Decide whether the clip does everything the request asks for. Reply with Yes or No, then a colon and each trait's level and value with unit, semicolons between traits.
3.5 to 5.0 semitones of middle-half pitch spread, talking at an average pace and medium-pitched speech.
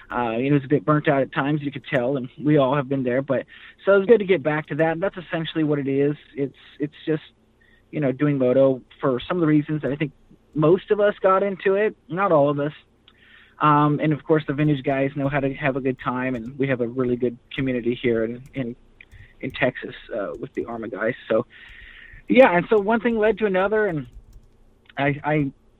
No: average, 4.1 semitones; fast, 235 wpm; medium, 145 Hz